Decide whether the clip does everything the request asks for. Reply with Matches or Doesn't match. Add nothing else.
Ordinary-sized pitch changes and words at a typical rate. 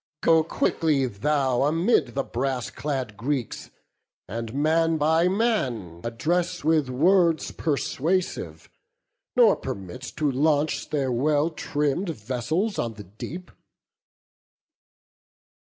Doesn't match